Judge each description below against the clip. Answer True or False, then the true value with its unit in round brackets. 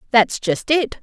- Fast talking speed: False (175 wpm)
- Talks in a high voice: True (245 Hz)